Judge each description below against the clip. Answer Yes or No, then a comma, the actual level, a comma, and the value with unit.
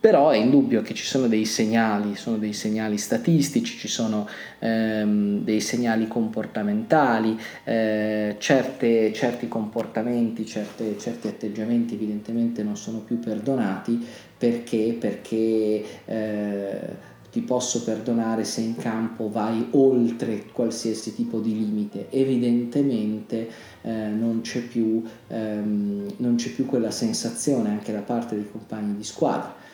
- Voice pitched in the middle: No, low, 110 Hz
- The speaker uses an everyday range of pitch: No, narrow, 1.6 semitones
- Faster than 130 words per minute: No, average, 125 wpm